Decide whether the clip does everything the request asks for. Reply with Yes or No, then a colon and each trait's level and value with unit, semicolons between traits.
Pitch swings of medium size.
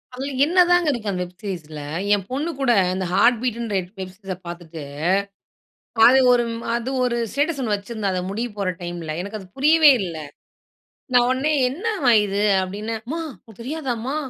No: wide, 6.0 semitones